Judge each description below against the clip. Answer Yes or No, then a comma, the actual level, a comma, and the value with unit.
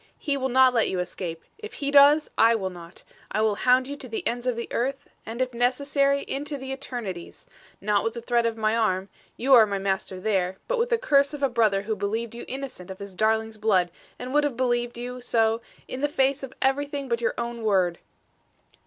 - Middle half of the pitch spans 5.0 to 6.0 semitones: No, average, 4.2 semitones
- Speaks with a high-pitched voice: Yes, high, 235 Hz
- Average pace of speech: No, fast, 220 wpm